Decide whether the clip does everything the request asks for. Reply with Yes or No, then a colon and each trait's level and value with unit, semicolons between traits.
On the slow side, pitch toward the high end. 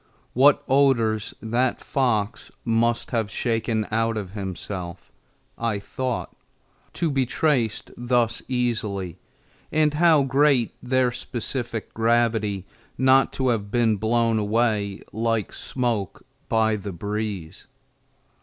No: slow, 110 wpm; low, 115 Hz